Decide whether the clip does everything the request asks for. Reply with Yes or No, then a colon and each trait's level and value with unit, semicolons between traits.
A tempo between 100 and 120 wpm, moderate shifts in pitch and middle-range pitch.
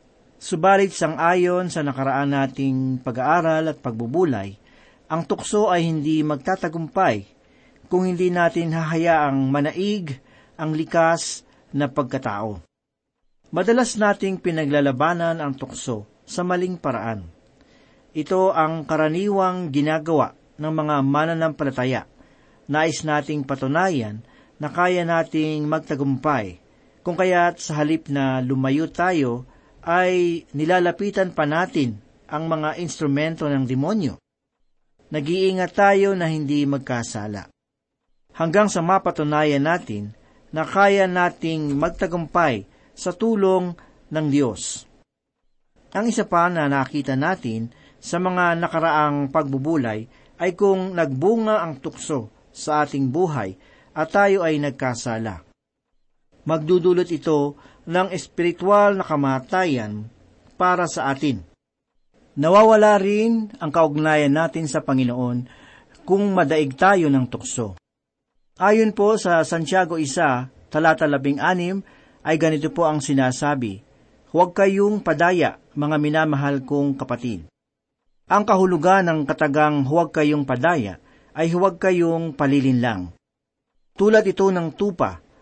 Yes: slow, 110 wpm; average, 4.6 semitones; medium, 155 Hz